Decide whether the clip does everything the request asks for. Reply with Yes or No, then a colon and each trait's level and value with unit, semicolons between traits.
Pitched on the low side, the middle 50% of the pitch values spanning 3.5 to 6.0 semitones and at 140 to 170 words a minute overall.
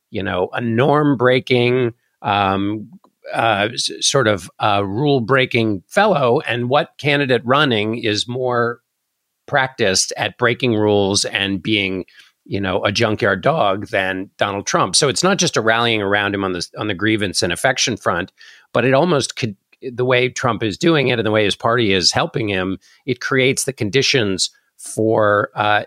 Yes: low, 115 Hz; average, 3.9 semitones; average, 165 wpm